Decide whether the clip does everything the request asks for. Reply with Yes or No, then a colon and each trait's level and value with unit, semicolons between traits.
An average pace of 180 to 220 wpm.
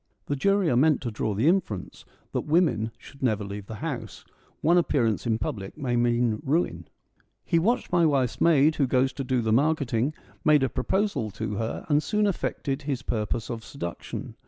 Yes: average, 190 wpm